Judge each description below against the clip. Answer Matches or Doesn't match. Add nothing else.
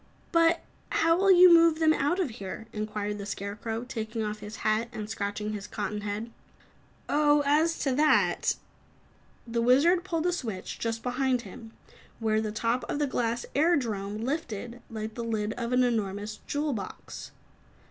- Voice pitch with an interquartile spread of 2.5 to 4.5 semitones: Doesn't match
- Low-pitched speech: Doesn't match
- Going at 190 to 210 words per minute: Doesn't match